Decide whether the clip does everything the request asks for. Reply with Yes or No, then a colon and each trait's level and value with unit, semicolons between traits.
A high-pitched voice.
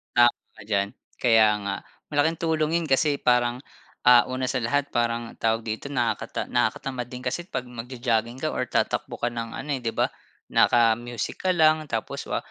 No: low, 120 Hz